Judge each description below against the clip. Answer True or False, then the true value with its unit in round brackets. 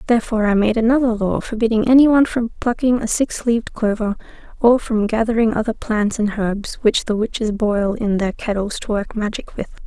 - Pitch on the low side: False (220 Hz)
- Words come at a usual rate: True (190 wpm)